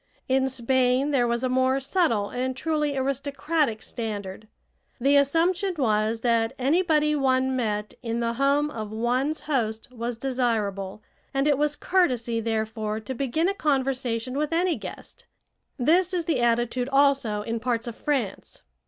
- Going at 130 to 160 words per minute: Yes, average, 150 wpm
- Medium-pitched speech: No, very high, 255 Hz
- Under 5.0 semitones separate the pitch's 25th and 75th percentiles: Yes, average, 3.9 semitones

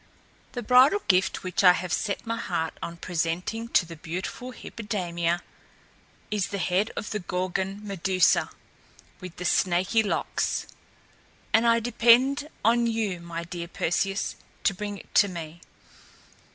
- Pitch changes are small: No, average, 4.4 semitones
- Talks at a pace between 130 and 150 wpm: Yes, average, 140 wpm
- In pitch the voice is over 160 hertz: Yes, high, 190 Hz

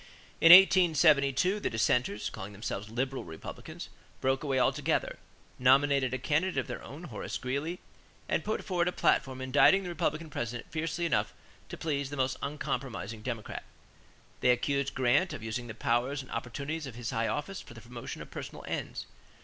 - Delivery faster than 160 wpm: Yes, average, 170 wpm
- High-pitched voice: No, low, 135 Hz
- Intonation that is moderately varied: Yes, average, 4.4 semitones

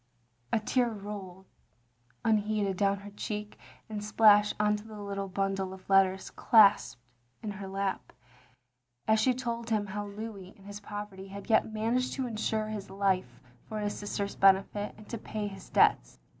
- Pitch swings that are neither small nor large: No, narrow, 1.8 semitones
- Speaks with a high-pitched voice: Yes, high, 205 Hz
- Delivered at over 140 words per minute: Yes, average, 165 wpm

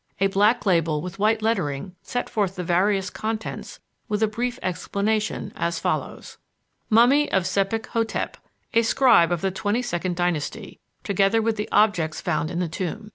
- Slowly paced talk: No, average, 165 wpm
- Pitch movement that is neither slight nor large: Yes, average, 3.8 semitones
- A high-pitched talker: Yes, high, 200 Hz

